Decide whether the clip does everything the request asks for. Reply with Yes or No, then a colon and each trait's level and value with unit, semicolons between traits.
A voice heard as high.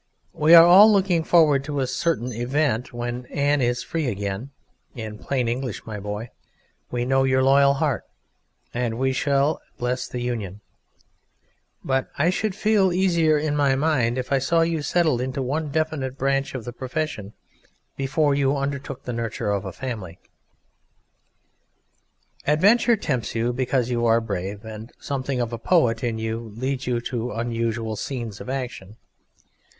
No: low, 130 Hz